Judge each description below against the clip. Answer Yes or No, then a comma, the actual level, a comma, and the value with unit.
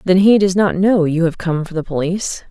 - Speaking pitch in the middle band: Yes, medium, 180 Hz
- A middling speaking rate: No, fast, 265 wpm